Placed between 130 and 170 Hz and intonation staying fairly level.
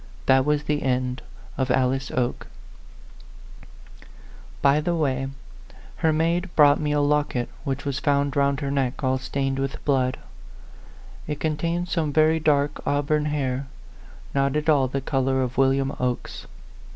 Yes: medium, 140 Hz; narrow, 2.1 semitones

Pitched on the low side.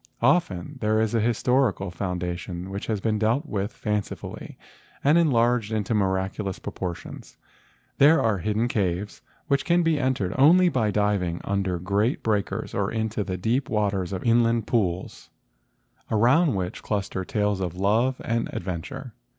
Yes: low, 105 Hz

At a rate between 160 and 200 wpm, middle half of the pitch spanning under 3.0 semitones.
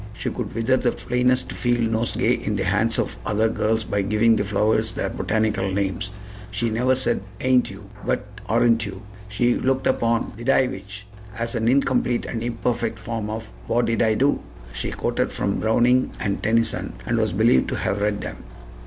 Yes: average, 185 wpm; narrow, 2.4 semitones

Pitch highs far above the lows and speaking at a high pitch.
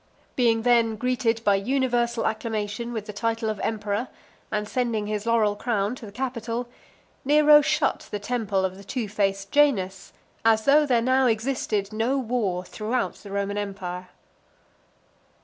No: average, 3.2 semitones; high, 225 Hz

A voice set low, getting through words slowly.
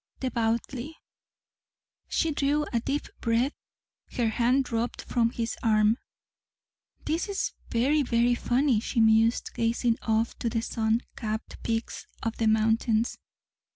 No: high, 235 Hz; slow, 125 wpm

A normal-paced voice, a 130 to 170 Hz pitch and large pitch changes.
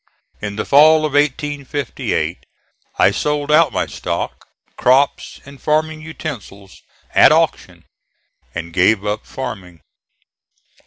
No: slow, 110 wpm; medium, 140 Hz; wide, 6.5 semitones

